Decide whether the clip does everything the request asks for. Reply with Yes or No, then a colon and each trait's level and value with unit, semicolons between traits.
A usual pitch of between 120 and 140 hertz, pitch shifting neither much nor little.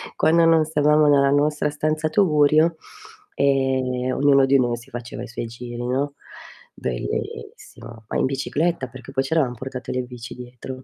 Yes: low, 135 Hz; average, 3.2 semitones